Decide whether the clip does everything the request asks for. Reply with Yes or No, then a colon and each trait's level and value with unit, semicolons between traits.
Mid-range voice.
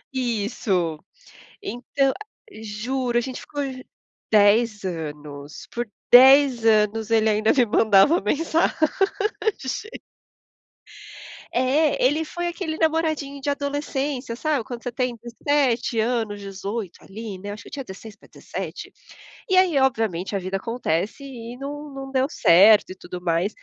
No: high, 235 Hz